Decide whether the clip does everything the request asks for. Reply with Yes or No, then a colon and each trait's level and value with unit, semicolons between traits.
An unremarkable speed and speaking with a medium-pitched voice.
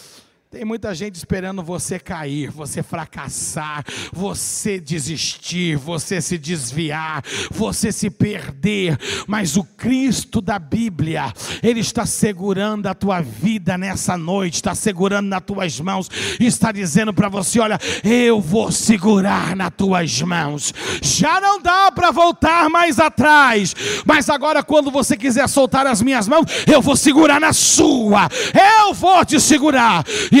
No: average, 140 wpm; high, 205 Hz